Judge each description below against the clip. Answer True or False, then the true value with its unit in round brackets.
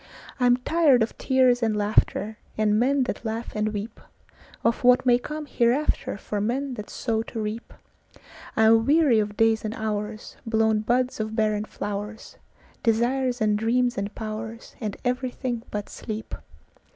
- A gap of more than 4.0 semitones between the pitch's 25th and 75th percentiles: False (2.6 semitones)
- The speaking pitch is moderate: False (225 Hz)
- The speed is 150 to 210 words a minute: False (135 wpm)